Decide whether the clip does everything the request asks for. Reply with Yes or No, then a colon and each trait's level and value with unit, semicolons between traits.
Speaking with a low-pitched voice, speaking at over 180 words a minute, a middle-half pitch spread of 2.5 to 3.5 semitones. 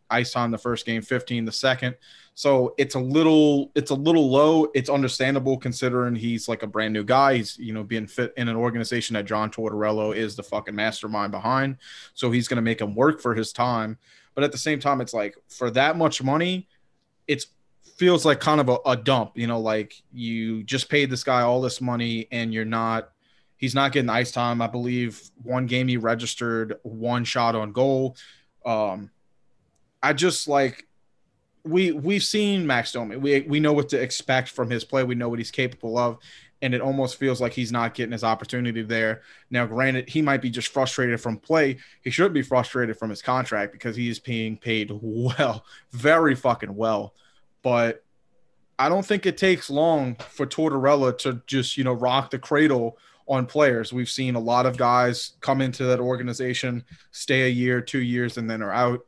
Yes: low, 125 Hz; average, 200 wpm; average, 2.8 semitones